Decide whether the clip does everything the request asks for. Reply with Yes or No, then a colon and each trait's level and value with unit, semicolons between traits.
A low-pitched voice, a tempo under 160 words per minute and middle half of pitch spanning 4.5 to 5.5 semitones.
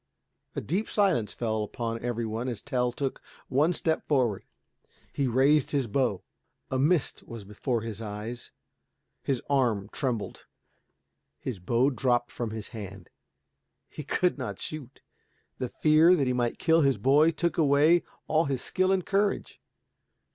Yes: low, 130 Hz; average, 150 wpm; average, 4.9 semitones